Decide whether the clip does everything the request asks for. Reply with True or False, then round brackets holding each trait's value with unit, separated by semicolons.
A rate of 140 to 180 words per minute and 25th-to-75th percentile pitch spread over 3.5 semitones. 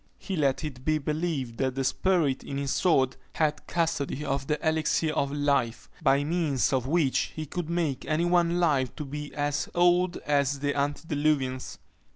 False (175 wpm; 2.9 semitones)